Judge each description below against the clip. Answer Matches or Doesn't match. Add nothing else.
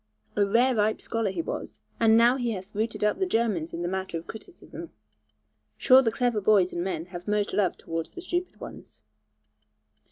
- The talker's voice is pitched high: Matches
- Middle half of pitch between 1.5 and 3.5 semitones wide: Doesn't match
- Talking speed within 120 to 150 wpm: Doesn't match